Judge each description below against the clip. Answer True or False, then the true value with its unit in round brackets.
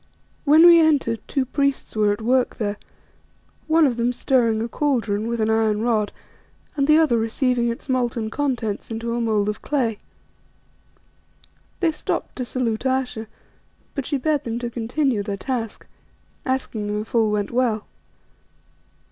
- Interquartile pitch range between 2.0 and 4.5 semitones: True (3.2 semitones)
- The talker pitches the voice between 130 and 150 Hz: False (235 Hz)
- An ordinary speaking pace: True (155 wpm)